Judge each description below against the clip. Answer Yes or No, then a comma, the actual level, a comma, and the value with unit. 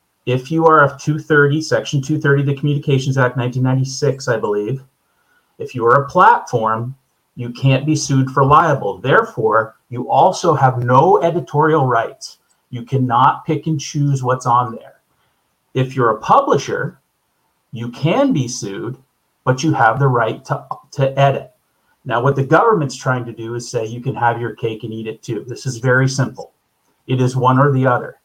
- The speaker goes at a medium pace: Yes, average, 180 wpm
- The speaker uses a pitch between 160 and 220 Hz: No, low, 135 Hz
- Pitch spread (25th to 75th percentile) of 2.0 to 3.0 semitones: Yes, average, 2.7 semitones